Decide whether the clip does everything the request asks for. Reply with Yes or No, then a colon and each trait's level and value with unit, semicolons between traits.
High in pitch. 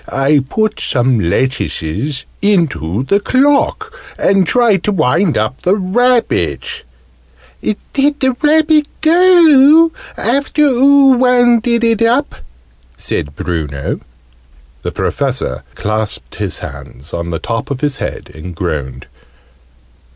Yes: high, 200 Hz